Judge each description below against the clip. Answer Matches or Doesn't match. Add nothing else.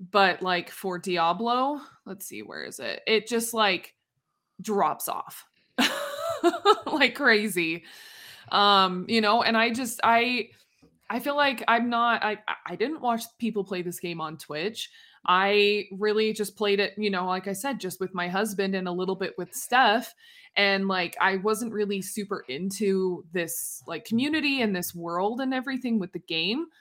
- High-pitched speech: Matches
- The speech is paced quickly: Doesn't match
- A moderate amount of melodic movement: Matches